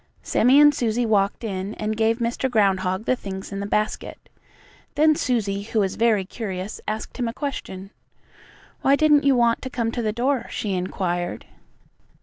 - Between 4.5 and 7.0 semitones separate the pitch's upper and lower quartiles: No, average, 3.9 semitones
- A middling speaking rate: Yes, average, 170 wpm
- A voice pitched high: Yes, high, 220 Hz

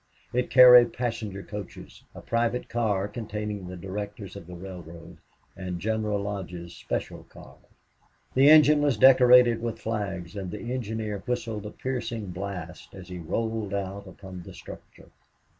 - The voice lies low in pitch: Yes, low, 105 Hz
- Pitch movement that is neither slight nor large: Yes, average, 3.7 semitones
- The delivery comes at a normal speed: Yes, average, 145 wpm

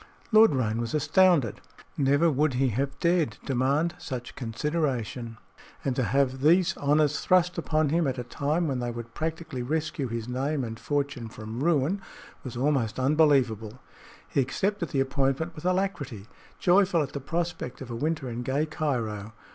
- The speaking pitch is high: No, medium, 140 Hz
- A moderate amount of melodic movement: Yes, average, 4.5 semitones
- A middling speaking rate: Yes, average, 165 wpm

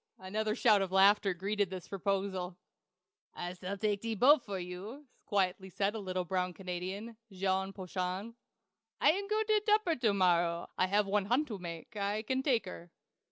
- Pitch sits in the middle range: No, high, 195 Hz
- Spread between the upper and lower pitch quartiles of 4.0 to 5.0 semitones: No, average, 2.9 semitones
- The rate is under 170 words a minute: No, average, 175 wpm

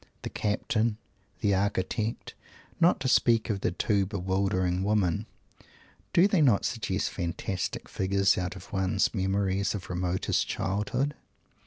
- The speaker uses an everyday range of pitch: No, narrow, 2.3 semitones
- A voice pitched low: Yes, low, 100 Hz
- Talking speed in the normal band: No, slow, 130 wpm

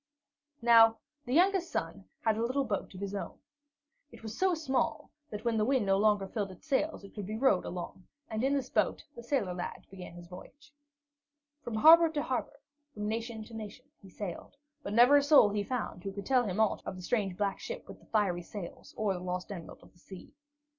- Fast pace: Yes, fast, 220 wpm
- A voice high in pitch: Yes, high, 220 Hz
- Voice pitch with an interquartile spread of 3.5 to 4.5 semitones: No, average, 5.1 semitones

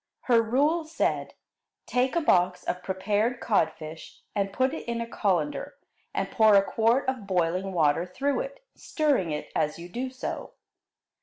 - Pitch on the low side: No, high, 220 Hz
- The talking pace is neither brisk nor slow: Yes, average, 160 wpm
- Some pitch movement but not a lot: No, wide, 6.4 semitones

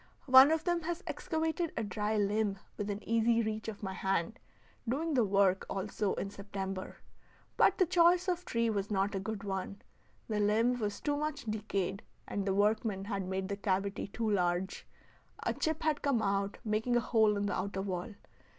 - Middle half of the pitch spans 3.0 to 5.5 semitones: Yes, average, 3.6 semitones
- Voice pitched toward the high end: Yes, high, 210 Hz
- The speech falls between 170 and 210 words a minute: Yes, average, 185 wpm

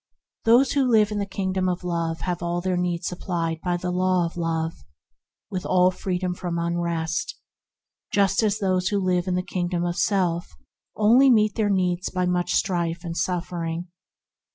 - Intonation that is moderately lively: No, narrow, 1.9 semitones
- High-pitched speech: No, medium, 180 Hz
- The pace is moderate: Yes, average, 175 wpm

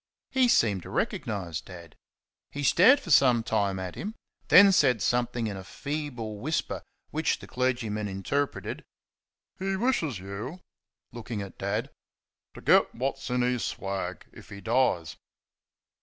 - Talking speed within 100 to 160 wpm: Yes, average, 145 wpm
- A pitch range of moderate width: No, wide, 6.3 semitones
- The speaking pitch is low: Yes, low, 120 Hz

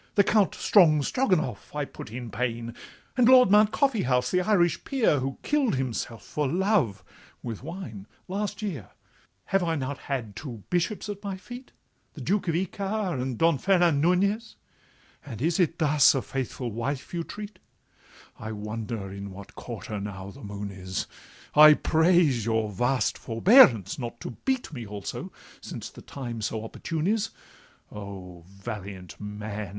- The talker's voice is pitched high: No, low, 135 Hz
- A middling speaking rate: Yes, average, 155 wpm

